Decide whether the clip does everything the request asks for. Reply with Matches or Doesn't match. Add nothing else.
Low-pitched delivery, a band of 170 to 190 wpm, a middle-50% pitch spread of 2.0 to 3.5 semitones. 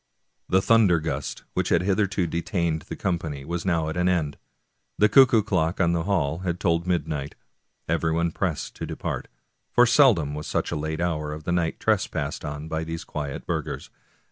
Matches